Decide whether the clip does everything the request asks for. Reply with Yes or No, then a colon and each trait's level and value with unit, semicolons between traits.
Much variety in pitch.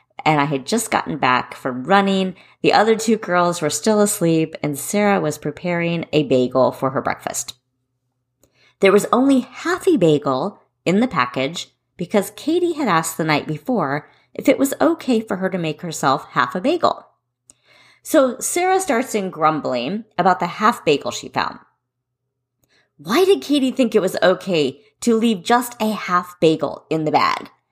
Yes: wide, 7.8 semitones